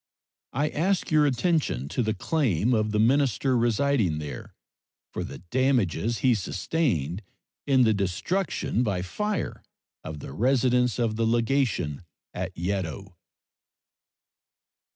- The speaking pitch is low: Yes, low, 115 Hz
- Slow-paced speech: Yes, slow, 120 wpm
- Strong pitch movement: Yes, wide, 6.3 semitones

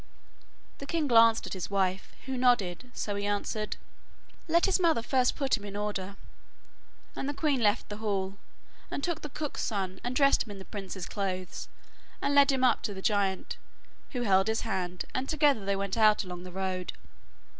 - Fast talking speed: No, average, 190 wpm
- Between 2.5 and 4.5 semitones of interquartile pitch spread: No, average, 5.3 semitones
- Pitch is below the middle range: No, high, 210 Hz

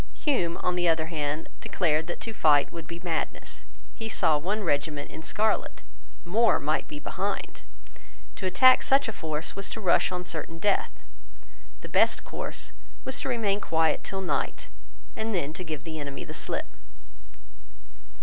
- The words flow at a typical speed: Yes, average, 165 wpm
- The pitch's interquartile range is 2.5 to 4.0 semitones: No, average, 4.5 semitones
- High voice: No, medium, 170 Hz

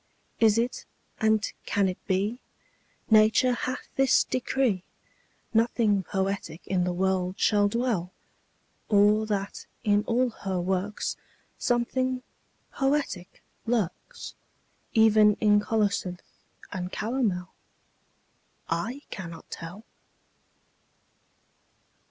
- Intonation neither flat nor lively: Yes, average, 3.7 semitones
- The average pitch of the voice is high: Yes, high, 210 Hz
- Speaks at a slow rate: Yes, slow, 90 wpm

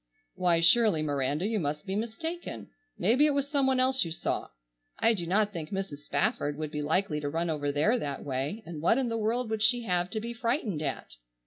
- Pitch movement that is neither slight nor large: No, wide, 7.3 semitones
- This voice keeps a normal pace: No, fast, 220 wpm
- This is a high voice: Yes, high, 195 Hz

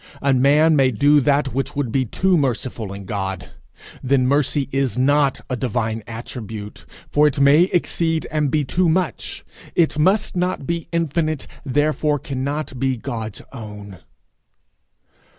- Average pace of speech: Yes, average, 145 wpm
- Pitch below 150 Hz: Yes, medium, 140 Hz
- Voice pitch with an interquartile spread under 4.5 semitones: Yes, average, 3.7 semitones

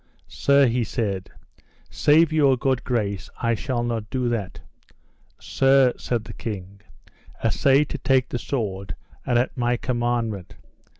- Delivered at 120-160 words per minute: Yes, slow, 135 wpm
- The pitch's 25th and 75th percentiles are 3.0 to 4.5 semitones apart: Yes, average, 3.5 semitones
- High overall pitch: No, low, 120 Hz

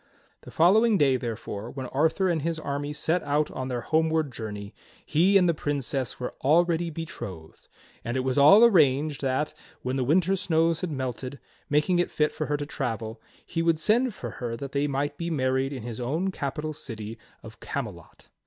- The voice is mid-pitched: Yes, medium, 145 Hz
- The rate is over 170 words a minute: Yes, average, 190 wpm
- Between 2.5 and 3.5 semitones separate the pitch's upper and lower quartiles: No, average, 4.3 semitones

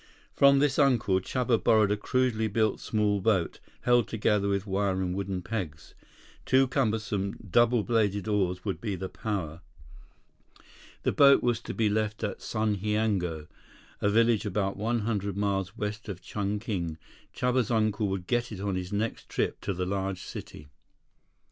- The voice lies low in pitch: Yes, low, 105 Hz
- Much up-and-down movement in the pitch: No, average, 2.7 semitones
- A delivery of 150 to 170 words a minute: Yes, average, 155 wpm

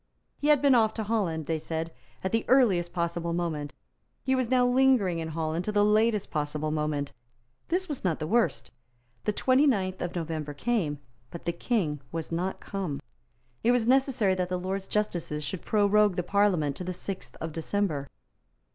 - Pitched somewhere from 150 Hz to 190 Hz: Yes, medium, 185 Hz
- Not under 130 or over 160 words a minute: No, average, 180 wpm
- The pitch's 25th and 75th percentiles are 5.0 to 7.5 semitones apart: Yes, wide, 5.4 semitones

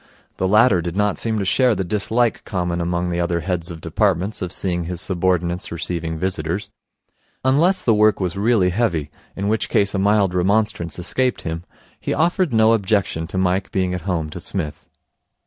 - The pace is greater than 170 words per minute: Yes, average, 180 wpm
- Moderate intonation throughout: Yes, average, 3.5 semitones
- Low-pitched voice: Yes, very low, 95 Hz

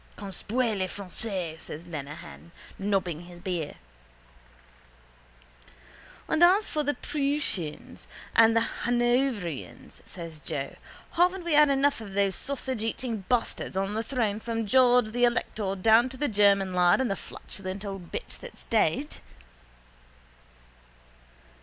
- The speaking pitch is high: Yes, high, 215 Hz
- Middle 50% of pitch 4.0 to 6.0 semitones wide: Yes, wide, 5.5 semitones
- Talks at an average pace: No, slow, 125 wpm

